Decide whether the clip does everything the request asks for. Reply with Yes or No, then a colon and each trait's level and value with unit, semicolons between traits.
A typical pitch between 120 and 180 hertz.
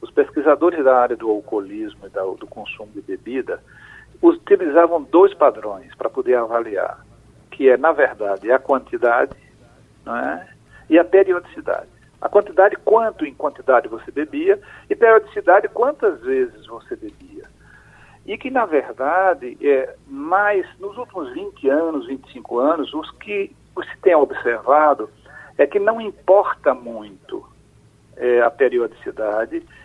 No: high, 220 Hz